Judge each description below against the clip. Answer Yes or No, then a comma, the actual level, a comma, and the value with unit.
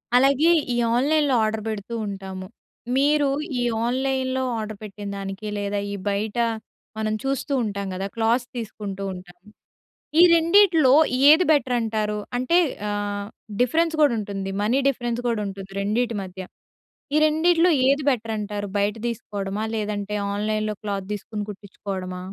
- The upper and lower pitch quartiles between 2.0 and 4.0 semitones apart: No, average, 4.5 semitones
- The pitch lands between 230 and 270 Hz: No, high, 215 Hz